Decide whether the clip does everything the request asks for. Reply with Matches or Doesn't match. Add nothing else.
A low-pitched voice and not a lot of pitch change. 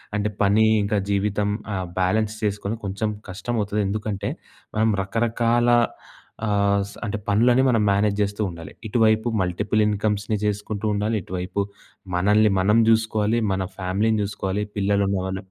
Matches